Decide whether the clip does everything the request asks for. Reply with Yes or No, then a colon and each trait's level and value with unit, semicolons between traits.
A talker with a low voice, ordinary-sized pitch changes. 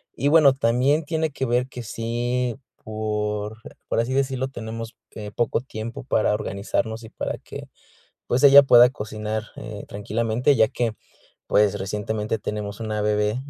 Yes: low, 115 Hz; average, 3.0 semitones